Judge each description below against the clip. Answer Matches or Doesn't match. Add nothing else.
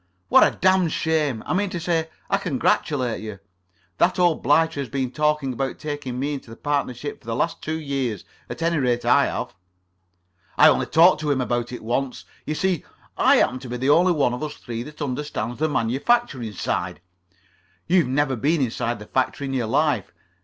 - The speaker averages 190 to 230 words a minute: Matches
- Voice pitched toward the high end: Doesn't match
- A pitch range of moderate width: Matches